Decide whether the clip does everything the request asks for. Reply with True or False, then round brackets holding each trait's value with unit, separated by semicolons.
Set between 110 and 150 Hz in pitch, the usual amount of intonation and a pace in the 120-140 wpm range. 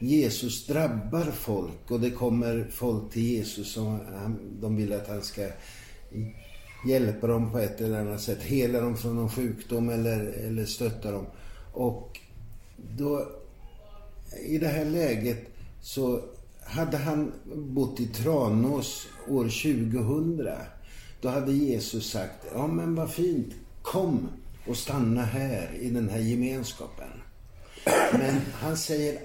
True (115 Hz; 3.8 semitones; 135 wpm)